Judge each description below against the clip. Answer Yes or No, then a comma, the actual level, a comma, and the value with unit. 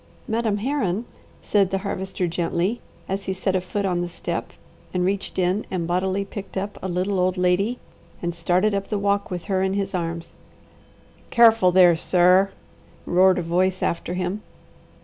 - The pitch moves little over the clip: Yes, narrow, 1.9 semitones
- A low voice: No, medium, 185 Hz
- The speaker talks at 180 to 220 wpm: No, average, 170 wpm